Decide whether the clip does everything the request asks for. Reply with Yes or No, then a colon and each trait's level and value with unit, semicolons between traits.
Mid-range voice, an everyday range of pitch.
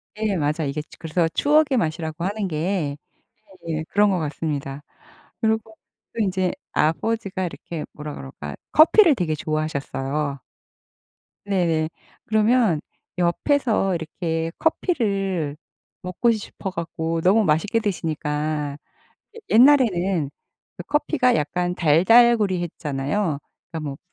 No: medium, 175 Hz; wide, 5.7 semitones